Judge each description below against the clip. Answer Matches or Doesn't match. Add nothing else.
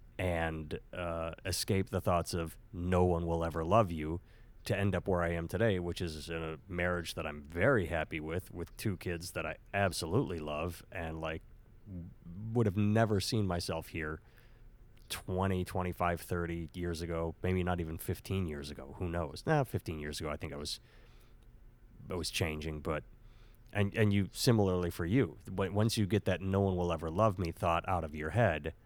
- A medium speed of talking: Matches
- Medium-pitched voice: Doesn't match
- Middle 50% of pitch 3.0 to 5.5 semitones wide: Matches